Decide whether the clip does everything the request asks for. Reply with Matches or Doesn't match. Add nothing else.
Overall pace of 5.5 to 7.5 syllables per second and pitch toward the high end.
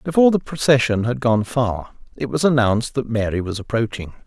Doesn't match